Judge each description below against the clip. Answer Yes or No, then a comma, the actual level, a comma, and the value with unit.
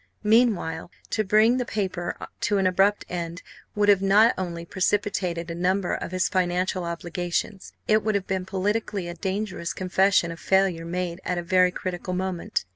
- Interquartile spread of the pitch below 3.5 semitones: Yes, narrow, 2.5 semitones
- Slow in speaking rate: No, average, 170 wpm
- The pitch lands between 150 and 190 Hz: Yes, medium, 185 Hz